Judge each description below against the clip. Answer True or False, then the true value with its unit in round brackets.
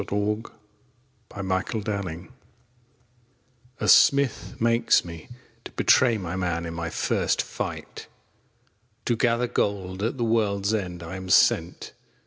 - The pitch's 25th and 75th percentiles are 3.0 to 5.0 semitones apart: True (3.9 semitones)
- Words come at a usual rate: False (130 wpm)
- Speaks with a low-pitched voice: True (100 Hz)